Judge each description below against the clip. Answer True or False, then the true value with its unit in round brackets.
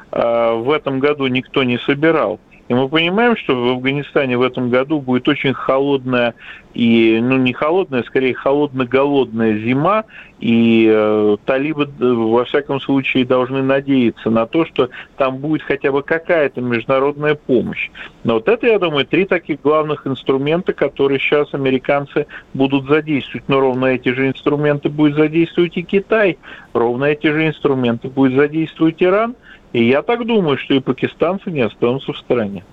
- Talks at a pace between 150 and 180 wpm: True (155 wpm)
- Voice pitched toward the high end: False (135 Hz)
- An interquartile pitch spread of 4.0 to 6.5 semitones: False (3.4 semitones)